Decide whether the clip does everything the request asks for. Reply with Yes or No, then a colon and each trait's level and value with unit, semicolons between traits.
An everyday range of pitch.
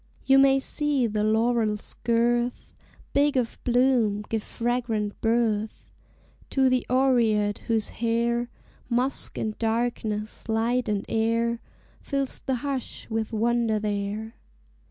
No: narrow, 2.3 semitones